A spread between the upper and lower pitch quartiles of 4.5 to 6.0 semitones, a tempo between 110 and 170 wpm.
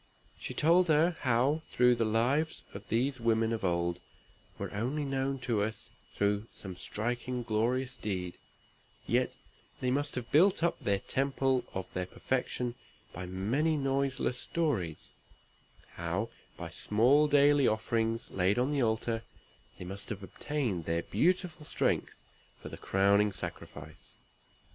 Yes: average, 5.3 semitones; average, 140 wpm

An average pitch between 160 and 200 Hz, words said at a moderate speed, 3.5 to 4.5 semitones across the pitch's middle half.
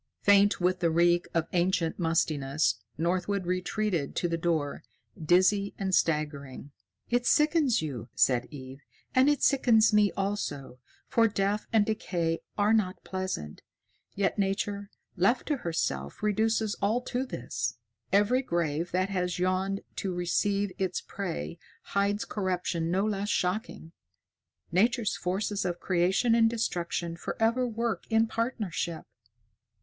No: high, 190 Hz; slow, 130 wpm; average, 4.0 semitones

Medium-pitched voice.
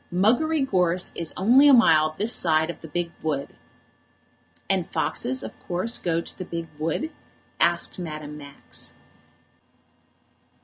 Yes: medium, 170 Hz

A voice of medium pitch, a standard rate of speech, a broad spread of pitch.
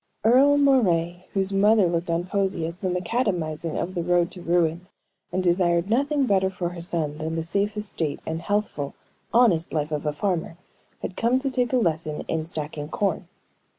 No: medium, 175 Hz; average, 185 wpm; average, 3.9 semitones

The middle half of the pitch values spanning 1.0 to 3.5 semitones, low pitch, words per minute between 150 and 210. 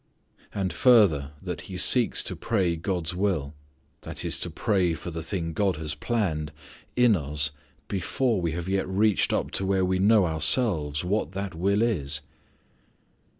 No: average, 4.1 semitones; very low, 90 Hz; average, 160 wpm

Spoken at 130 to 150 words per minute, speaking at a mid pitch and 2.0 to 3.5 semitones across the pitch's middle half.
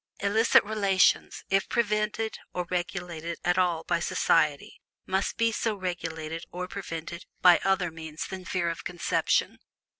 Yes: average, 140 wpm; medium, 180 Hz; average, 2.9 semitones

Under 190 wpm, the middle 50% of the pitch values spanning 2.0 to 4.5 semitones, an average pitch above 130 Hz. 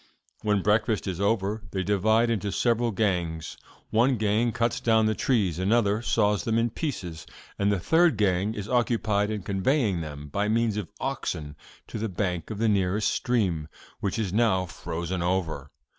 No: average, 170 wpm; average, 3.5 semitones; low, 105 Hz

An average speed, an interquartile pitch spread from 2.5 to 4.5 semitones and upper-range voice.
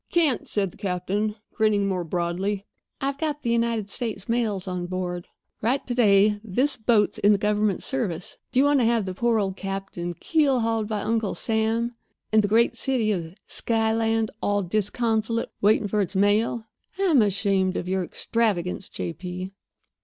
Yes: average, 170 wpm; average, 3.2 semitones; high, 210 Hz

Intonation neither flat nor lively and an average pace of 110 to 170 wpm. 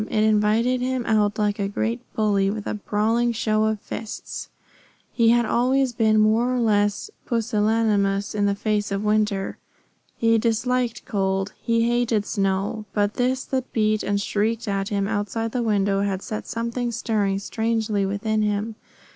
No: narrow, 2.2 semitones; average, 160 wpm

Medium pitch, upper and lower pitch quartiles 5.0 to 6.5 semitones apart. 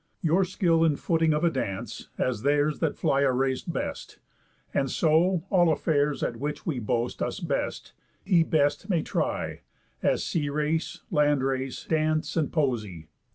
No: medium, 150 Hz; average, 3.4 semitones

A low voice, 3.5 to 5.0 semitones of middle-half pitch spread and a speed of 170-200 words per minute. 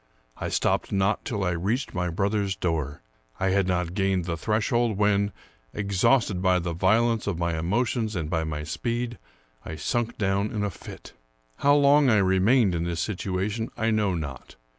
Yes: low, 100 Hz; average, 4.1 semitones; average, 175 wpm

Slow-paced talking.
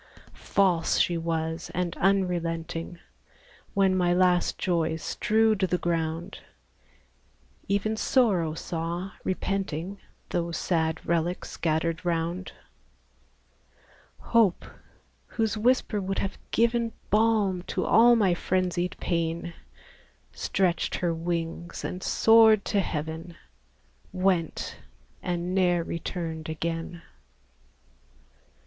Yes: slow, 95 wpm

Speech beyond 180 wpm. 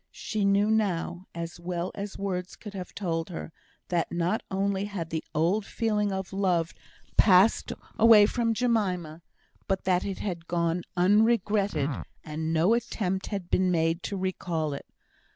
No: average, 150 wpm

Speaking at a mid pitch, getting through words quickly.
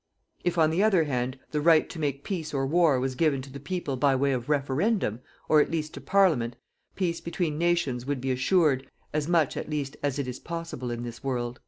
Yes: medium, 145 Hz; fast, 220 wpm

